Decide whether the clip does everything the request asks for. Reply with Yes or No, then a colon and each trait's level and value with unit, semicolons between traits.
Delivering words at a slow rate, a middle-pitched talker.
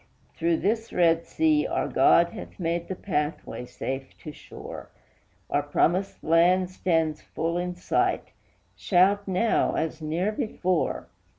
Yes: slow, 130 wpm; medium, 175 Hz